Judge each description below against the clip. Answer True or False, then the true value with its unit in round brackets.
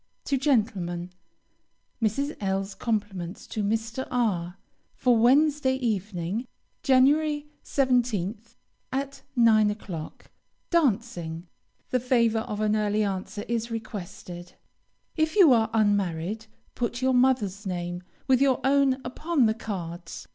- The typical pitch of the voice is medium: False (225 Hz)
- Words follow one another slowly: True (120 wpm)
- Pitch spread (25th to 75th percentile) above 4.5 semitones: True (5.0 semitones)